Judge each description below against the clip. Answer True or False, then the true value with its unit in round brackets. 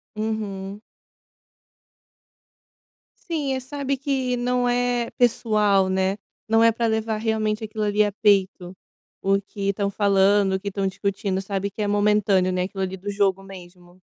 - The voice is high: True (205 Hz)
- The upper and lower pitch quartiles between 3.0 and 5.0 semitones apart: False (2.5 semitones)